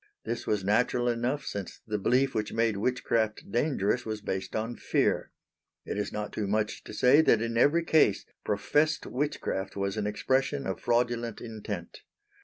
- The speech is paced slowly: No, average, 165 wpm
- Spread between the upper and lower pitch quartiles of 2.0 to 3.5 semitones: Yes, average, 3.1 semitones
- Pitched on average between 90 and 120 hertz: Yes, low, 115 Hz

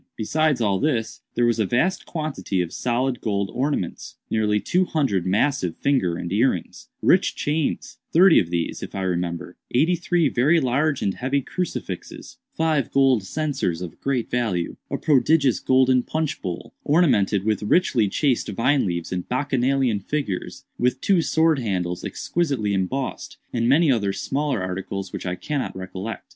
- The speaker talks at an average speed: Yes, average, 155 wpm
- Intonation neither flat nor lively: No, wide, 6.9 semitones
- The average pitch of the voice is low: Yes, low, 125 Hz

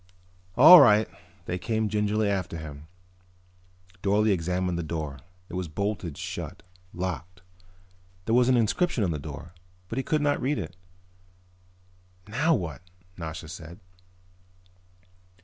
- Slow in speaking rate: Yes, slow, 130 wpm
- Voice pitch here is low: Yes, very low, 95 Hz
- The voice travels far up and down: No, average, 4.9 semitones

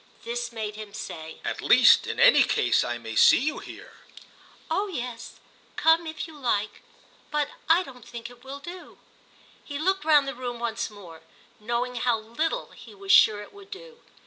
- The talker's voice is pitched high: Yes, very high, 250 Hz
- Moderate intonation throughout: No, wide, 6.3 semitones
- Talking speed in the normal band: Yes, average, 180 wpm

